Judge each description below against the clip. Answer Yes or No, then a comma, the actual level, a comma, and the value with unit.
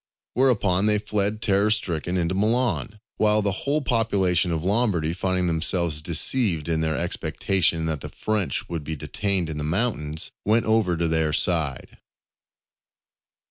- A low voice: Yes, very low, 95 Hz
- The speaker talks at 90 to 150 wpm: Yes, average, 145 wpm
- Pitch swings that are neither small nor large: Yes, average, 4.7 semitones